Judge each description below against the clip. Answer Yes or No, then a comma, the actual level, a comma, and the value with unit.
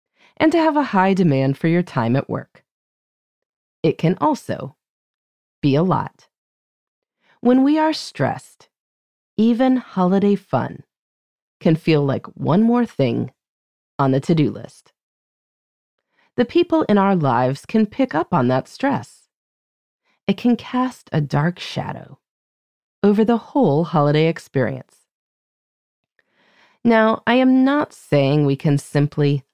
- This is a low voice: No, high, 195 Hz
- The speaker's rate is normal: No, slow, 130 wpm